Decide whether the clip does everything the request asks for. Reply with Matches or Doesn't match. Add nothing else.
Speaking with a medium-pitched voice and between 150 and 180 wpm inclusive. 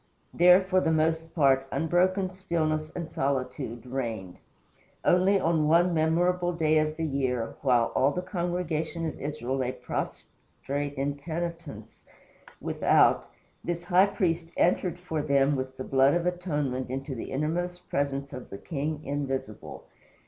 Doesn't match